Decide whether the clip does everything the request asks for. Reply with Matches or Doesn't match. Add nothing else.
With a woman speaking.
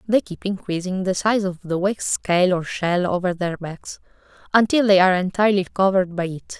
Matches